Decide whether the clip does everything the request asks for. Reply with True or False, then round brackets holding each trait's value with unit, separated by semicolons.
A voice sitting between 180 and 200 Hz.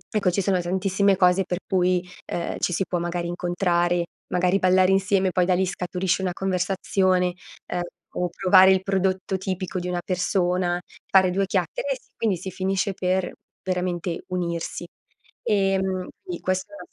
True (185 Hz)